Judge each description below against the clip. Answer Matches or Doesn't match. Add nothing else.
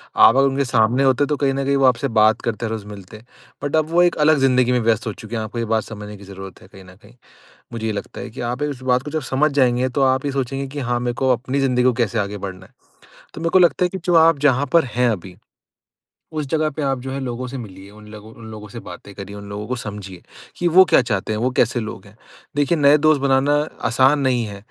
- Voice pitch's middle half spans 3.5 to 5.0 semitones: Matches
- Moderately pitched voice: Doesn't match